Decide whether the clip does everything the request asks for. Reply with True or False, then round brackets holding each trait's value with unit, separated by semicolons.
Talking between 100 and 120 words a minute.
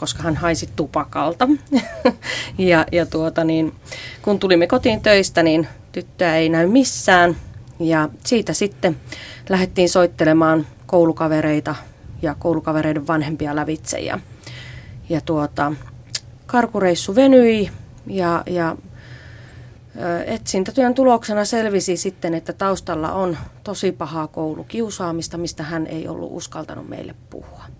True (110 wpm)